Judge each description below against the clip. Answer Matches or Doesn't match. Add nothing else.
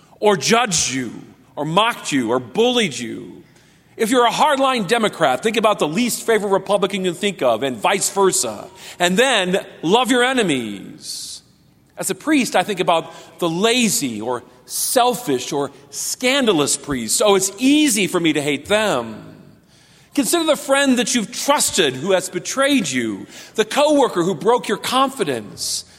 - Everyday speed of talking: Matches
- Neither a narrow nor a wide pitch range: Doesn't match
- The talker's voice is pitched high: Matches